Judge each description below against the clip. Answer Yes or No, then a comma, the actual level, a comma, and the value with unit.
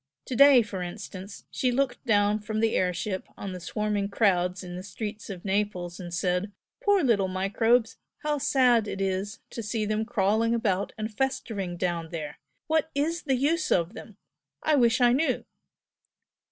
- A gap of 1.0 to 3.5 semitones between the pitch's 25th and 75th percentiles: No, average, 4.4 semitones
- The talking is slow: No, average, 175 wpm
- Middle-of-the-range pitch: No, high, 210 Hz